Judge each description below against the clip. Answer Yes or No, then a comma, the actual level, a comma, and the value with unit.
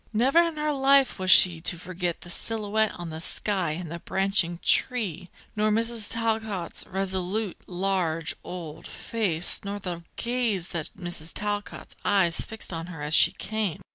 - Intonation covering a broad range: No, average, 4.1 semitones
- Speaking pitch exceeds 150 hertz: Yes, high, 190 Hz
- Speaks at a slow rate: No, average, 160 wpm